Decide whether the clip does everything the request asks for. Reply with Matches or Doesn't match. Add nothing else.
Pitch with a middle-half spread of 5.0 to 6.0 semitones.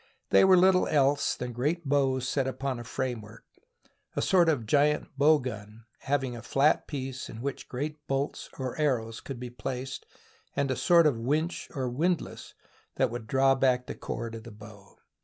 Doesn't match